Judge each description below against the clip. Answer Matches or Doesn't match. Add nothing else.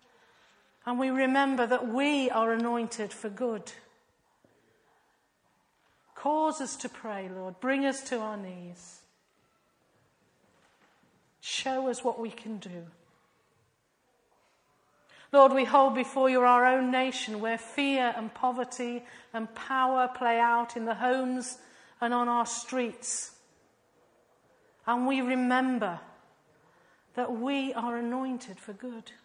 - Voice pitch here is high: Matches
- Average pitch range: Doesn't match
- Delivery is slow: Matches